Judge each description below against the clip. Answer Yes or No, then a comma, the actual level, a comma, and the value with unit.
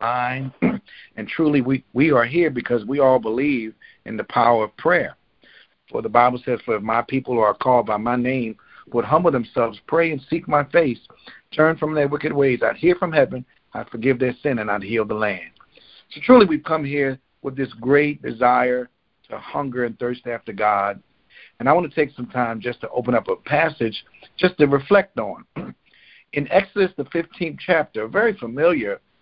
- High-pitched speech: No, low, 135 Hz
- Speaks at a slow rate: No, average, 195 wpm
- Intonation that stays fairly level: No, average, 4.2 semitones